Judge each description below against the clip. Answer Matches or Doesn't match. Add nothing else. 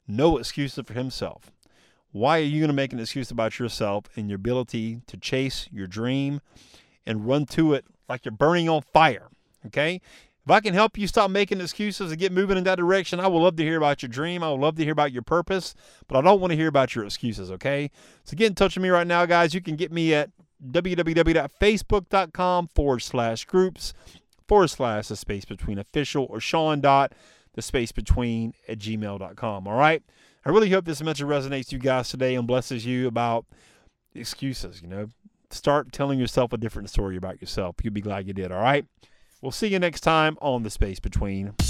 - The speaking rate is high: Matches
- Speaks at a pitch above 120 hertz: Matches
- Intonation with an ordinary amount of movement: Doesn't match